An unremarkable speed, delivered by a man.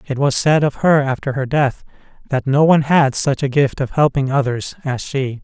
No: fast, 220 wpm; male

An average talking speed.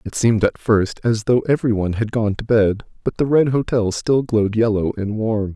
No: fast, 215 wpm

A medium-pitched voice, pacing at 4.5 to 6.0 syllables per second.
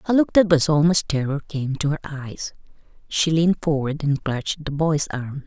Yes: medium, 150 Hz; 5.1 syllables/s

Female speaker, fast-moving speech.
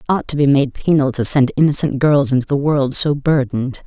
Yes: female; fast, 235 wpm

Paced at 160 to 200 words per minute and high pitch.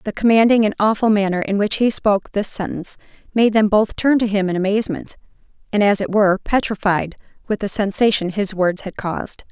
Yes: average, 195 wpm; high, 205 Hz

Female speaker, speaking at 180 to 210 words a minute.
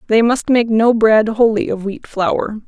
Yes: female; average, 200 wpm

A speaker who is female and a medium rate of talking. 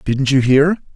No: male; average, 190 wpm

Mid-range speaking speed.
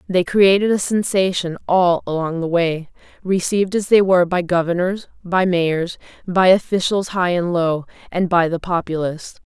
Yes: average, 160 wpm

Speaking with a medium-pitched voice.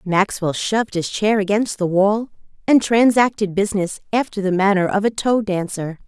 No: high, 200 Hz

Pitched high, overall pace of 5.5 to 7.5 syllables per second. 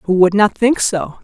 No: high, 200 Hz; 4.4 syllables/s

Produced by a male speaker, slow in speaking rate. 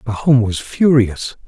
Yes: male; slow, 120 wpm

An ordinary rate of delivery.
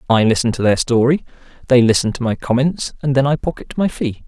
No: fast, 225 wpm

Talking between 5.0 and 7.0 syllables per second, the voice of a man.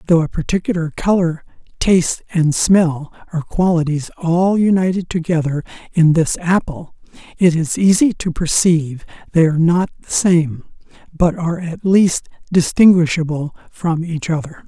No: 4.8 syllables/s; male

